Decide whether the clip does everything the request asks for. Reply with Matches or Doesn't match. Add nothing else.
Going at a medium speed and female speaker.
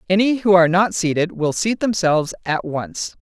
Matches